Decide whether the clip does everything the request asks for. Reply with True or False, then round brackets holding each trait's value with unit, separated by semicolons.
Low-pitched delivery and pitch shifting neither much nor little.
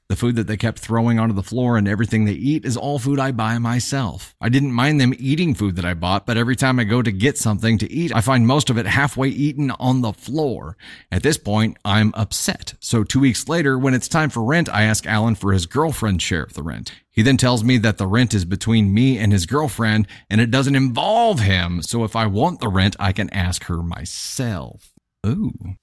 True (115 Hz; 4.5 semitones)